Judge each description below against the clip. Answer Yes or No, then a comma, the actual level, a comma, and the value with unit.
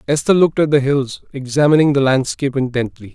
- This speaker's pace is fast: No, average, 170 wpm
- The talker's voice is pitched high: No, medium, 140 Hz